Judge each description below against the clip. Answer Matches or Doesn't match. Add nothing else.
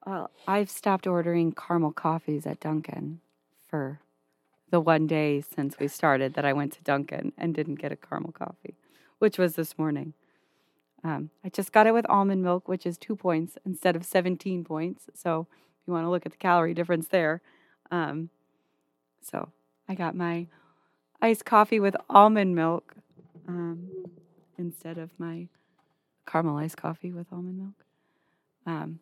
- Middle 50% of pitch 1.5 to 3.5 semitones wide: Matches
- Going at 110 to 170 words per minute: Matches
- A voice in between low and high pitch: Matches